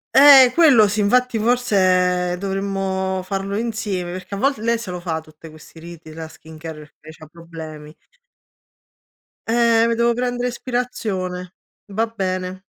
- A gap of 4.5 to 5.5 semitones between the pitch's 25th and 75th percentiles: Yes, average, 4.8 semitones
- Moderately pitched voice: No, high, 195 Hz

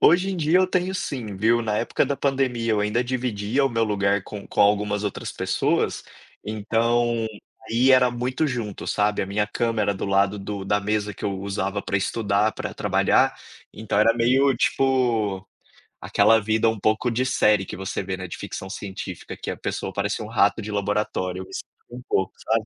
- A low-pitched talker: Yes, low, 110 Hz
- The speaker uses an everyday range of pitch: Yes, average, 3.1 semitones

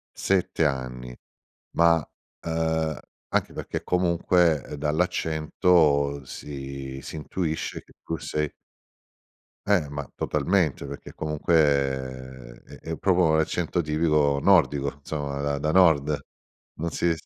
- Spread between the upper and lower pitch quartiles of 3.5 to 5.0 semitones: No, average, 2.9 semitones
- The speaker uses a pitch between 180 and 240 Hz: No, very low, 75 Hz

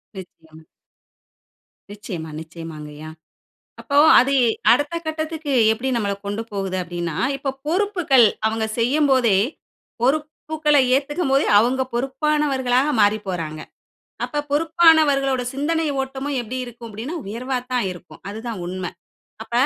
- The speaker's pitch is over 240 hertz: Yes, very high, 255 Hz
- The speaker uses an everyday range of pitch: No, wide, 6.5 semitones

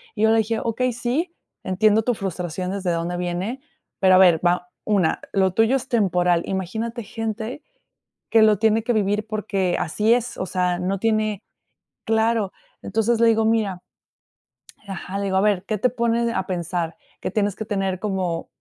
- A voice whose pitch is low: No, high, 205 Hz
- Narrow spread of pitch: No, average, 3.4 semitones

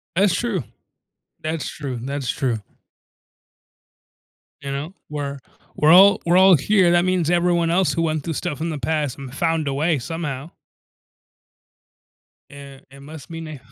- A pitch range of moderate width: Yes, average, 3.7 semitones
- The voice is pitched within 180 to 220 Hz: No, medium, 155 Hz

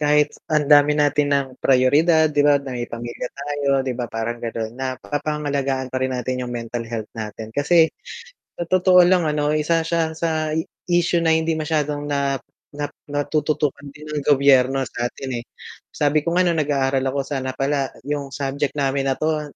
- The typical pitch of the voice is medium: Yes, medium, 145 Hz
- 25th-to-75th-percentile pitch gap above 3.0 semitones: No, narrow, 2.6 semitones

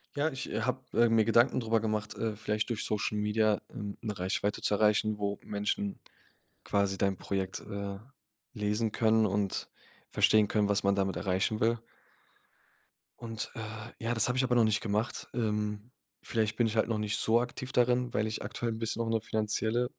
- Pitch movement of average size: No, narrow, 1.7 semitones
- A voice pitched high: No, low, 110 Hz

